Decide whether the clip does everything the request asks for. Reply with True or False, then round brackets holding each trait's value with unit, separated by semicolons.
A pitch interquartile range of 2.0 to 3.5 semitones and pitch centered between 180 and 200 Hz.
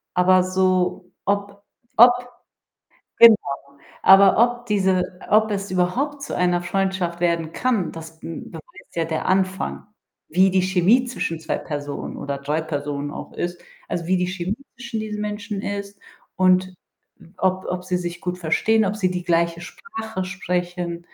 True (2.6 semitones; 185 Hz)